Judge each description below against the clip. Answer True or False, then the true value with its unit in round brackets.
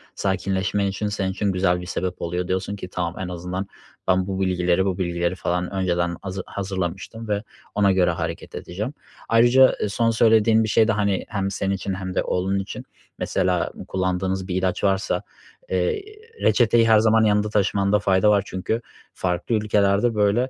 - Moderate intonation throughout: False (2.3 semitones)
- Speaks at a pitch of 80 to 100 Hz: True (95 Hz)